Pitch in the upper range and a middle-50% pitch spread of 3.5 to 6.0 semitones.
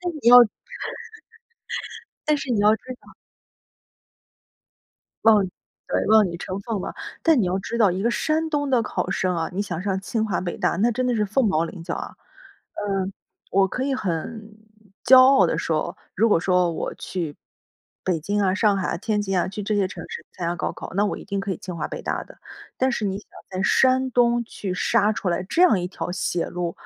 Yes: high, 205 Hz; average, 4.3 semitones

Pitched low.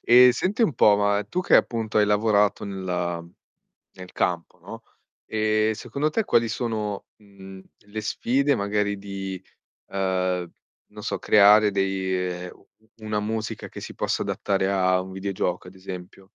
Yes: low, 100 Hz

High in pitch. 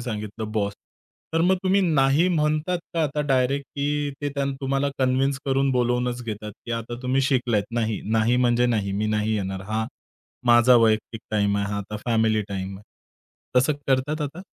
No: low, 125 Hz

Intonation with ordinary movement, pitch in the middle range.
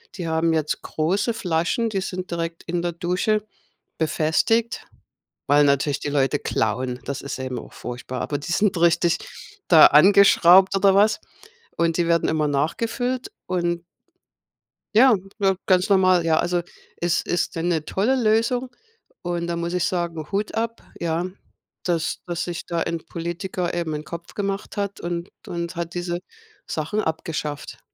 Yes: average, 3.1 semitones; medium, 170 Hz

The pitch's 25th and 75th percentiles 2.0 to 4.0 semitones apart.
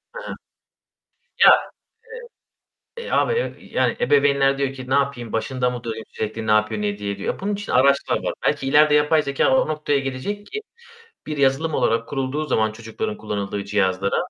No: average, 5.3 semitones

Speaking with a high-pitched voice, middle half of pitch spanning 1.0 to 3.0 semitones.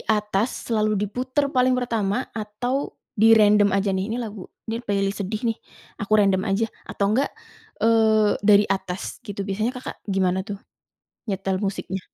Yes: high, 210 Hz; narrow, 2.4 semitones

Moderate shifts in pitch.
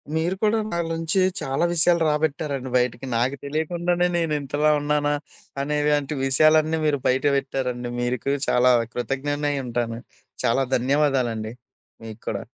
Yes: average, 3.6 semitones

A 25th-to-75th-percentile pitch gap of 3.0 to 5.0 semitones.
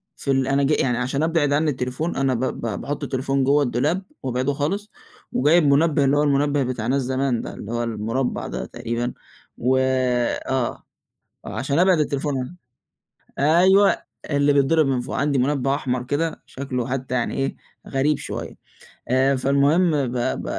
No: narrow, 2.4 semitones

